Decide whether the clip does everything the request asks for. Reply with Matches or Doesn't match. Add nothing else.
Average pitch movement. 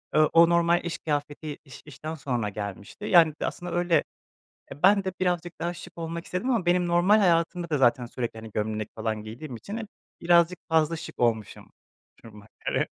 Doesn't match